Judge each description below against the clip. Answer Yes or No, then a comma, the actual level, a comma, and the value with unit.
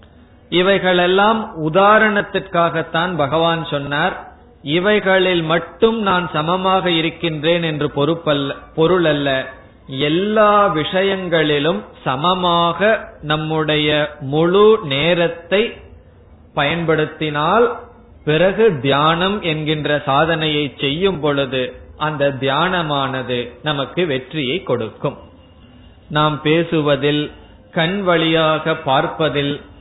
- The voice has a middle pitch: Yes, medium, 160 Hz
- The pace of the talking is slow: Yes, slow, 70 wpm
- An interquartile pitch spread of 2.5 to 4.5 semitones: Yes, average, 3.8 semitones